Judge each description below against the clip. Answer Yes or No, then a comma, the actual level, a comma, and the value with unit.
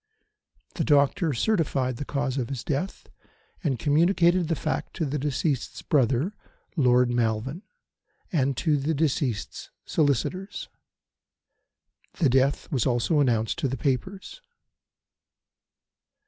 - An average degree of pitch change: Yes, average, 4.0 semitones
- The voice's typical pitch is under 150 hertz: Yes, medium, 140 Hz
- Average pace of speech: No, slow, 115 wpm